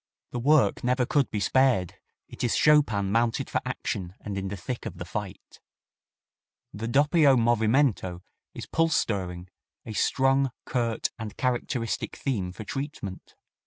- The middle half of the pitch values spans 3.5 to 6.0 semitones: Yes, average, 5.1 semitones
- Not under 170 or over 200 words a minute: No, average, 145 wpm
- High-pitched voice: No, low, 115 Hz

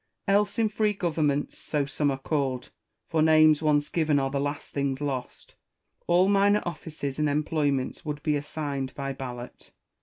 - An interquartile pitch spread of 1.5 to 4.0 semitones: Yes, average, 2.7 semitones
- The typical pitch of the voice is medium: Yes, medium, 150 Hz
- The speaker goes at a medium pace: Yes, average, 160 wpm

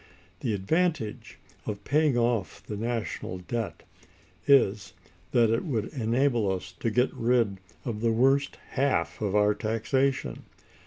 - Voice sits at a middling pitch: No, low, 115 Hz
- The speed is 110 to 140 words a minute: Yes, slow, 135 wpm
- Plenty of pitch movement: No, average, 4.0 semitones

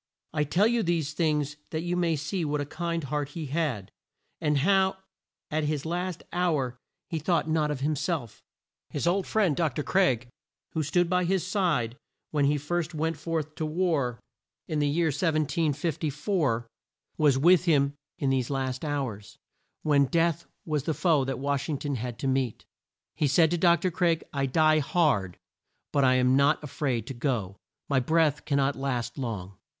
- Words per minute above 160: Yes, average, 180 wpm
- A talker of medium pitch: Yes, medium, 150 Hz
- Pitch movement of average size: Yes, average, 3.7 semitones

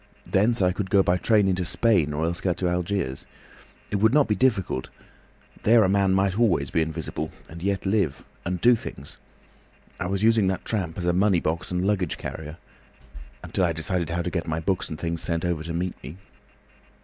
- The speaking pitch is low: Yes, very low, 90 Hz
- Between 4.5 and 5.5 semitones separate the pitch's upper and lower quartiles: No, average, 3.2 semitones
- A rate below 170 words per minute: No, average, 200 wpm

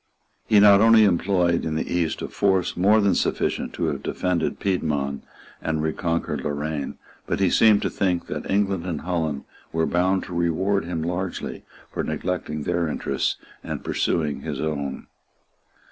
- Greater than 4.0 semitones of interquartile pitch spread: No, average, 3.5 semitones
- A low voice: Yes, very low, 85 Hz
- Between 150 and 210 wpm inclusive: Yes, average, 160 wpm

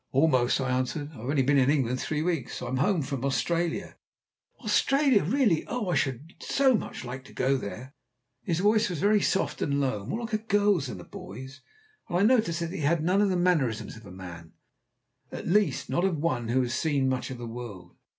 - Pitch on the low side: No, medium, 145 Hz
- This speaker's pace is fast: Yes, fast, 215 wpm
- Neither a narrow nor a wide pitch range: No, wide, 6.6 semitones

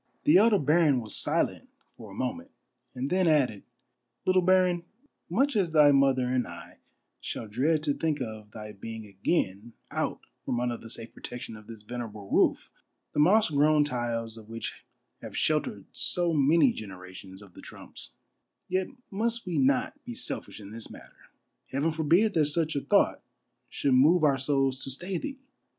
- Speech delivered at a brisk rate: No, average, 170 wpm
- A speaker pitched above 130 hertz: Yes, medium, 140 Hz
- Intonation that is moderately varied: No, wide, 7.1 semitones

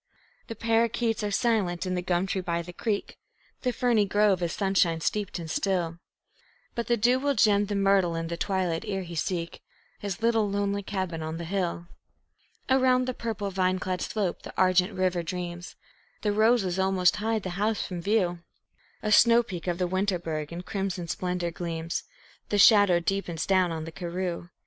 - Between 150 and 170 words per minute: No, average, 180 wpm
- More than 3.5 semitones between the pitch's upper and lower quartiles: No, average, 3.2 semitones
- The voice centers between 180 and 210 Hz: Yes, high, 190 Hz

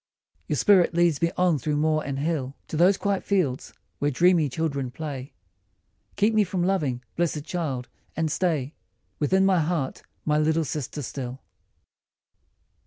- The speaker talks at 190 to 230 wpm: No, average, 155 wpm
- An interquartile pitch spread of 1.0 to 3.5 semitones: No, average, 4.0 semitones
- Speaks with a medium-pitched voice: Yes, medium, 155 Hz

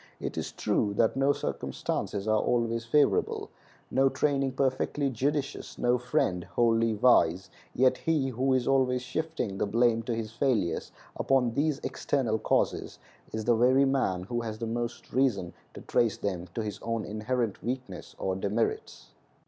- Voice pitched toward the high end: No, low, 120 Hz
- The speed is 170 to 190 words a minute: No, average, 155 wpm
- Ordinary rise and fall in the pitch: Yes, average, 3.5 semitones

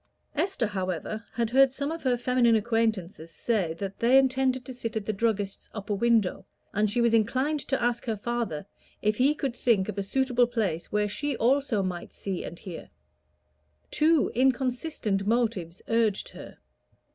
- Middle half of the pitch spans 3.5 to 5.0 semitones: Yes, average, 4.1 semitones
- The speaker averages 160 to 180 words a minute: Yes, average, 170 wpm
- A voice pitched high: Yes, high, 230 Hz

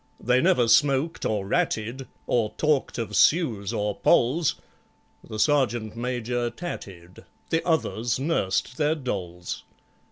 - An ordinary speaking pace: No, slow, 120 wpm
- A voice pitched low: Yes, low, 120 Hz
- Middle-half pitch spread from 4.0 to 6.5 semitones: Yes, average, 5.1 semitones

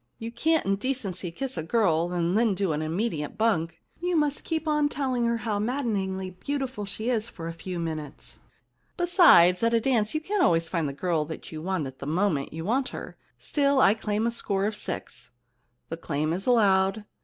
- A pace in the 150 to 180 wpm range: No, average, 200 wpm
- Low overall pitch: No, high, 200 Hz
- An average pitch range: No, wide, 6.5 semitones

